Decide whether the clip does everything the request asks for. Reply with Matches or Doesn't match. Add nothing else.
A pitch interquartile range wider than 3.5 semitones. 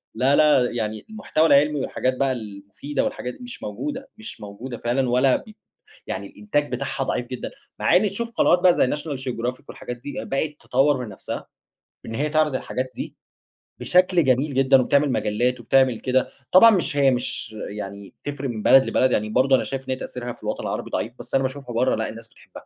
Doesn't match